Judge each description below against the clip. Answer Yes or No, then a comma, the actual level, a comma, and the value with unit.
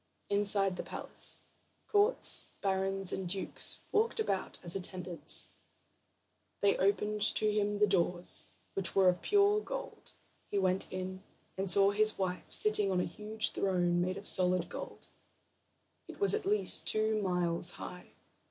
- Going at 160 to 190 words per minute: No, average, 150 wpm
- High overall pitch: Yes, high, 195 Hz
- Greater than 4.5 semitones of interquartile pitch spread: No, average, 2.7 semitones